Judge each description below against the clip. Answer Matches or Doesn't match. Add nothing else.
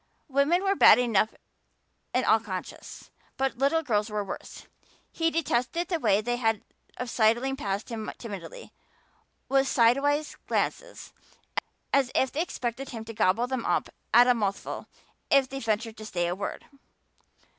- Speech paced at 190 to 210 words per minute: Doesn't match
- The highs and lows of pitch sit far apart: Doesn't match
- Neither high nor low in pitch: Doesn't match